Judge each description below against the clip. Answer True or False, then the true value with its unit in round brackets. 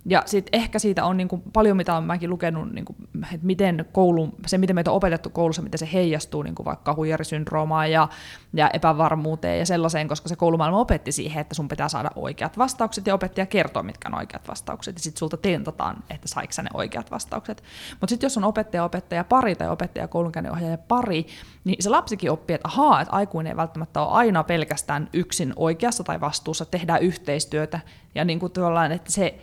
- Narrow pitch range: False (3.2 semitones)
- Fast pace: True (195 wpm)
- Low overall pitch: False (170 Hz)